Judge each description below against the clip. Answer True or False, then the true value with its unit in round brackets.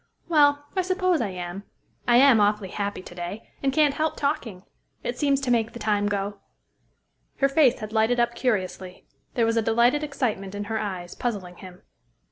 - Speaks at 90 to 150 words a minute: False (185 wpm)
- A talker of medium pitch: False (225 Hz)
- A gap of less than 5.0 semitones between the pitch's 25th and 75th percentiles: False (5.4 semitones)